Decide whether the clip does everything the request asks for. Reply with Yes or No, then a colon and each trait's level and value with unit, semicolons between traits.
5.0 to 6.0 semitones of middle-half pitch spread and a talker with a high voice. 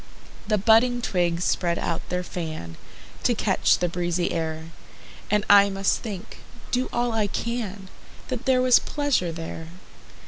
Yes: average, 5.3 semitones; high, 195 Hz